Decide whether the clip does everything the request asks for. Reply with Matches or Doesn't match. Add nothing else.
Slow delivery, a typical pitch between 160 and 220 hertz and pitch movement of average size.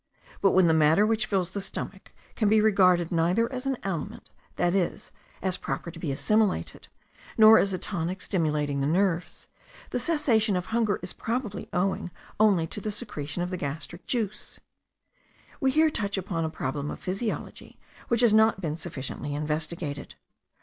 Doesn't match